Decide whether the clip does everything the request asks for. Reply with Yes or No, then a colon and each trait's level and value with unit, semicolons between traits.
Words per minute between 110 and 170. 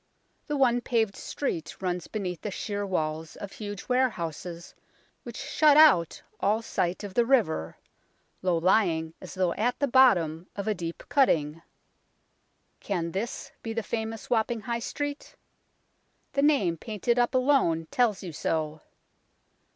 Yes: average, 145 wpm